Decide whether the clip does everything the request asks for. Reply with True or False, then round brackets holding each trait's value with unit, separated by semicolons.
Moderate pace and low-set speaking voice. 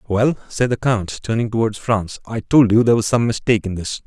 False (235 wpm; 110 Hz)